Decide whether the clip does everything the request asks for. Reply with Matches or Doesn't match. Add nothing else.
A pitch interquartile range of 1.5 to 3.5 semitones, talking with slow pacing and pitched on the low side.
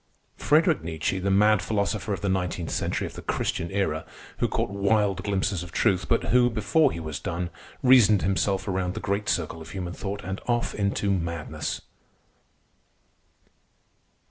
Doesn't match